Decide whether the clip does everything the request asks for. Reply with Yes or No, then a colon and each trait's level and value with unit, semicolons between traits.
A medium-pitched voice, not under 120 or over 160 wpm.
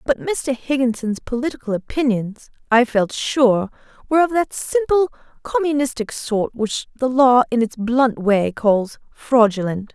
No: high, 245 Hz; average, 140 wpm